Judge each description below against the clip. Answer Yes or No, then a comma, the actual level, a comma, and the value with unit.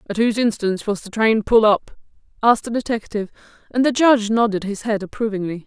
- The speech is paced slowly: No, average, 190 wpm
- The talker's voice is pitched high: Yes, high, 215 Hz